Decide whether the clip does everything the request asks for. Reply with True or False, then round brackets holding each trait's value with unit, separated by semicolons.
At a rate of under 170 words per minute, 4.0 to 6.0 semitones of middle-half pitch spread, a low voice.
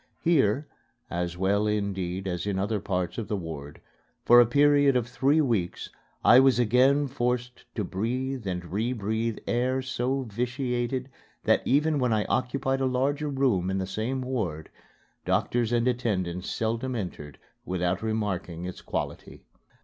True (150 wpm; 5.3 semitones; 115 Hz)